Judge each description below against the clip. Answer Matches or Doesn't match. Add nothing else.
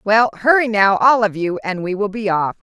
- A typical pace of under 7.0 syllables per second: Matches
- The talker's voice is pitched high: Matches